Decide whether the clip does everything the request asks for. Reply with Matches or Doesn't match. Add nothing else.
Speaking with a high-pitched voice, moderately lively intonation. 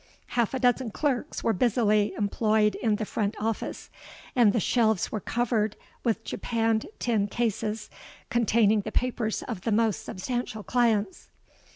Doesn't match